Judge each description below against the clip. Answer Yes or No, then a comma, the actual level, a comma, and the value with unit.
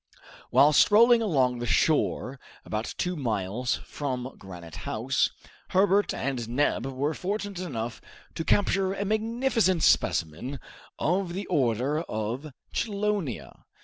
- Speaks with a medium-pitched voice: Yes, medium, 145 Hz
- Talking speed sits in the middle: No, slow, 115 wpm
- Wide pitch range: Yes, wide, 8.2 semitones